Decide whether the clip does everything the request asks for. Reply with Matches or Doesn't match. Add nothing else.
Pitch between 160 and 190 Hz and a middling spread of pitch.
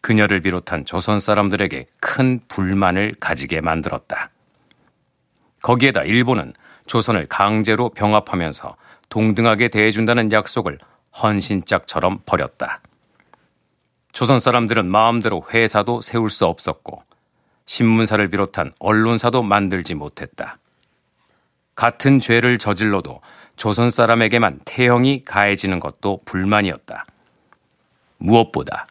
Doesn't match